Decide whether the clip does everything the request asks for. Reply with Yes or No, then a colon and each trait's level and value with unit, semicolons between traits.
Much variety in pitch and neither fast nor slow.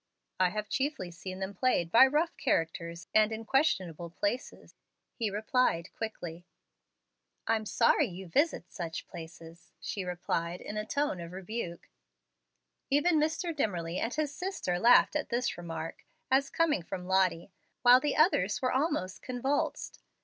Yes: wide, 7.3 semitones; average, 145 wpm